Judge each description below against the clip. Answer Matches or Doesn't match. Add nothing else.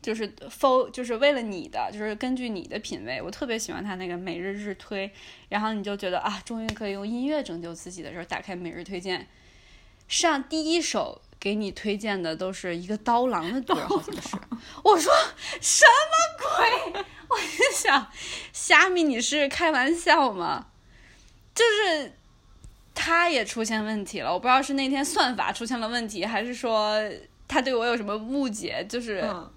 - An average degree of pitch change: Doesn't match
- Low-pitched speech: Doesn't match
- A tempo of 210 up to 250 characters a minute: Doesn't match